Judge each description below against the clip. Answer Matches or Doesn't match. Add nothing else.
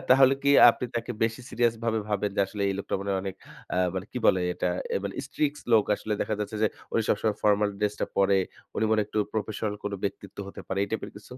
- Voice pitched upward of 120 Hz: Doesn't match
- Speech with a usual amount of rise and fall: Doesn't match